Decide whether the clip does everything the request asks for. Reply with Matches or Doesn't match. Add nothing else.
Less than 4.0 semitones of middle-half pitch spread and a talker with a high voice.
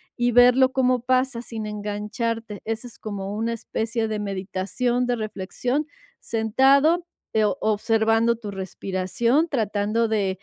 Matches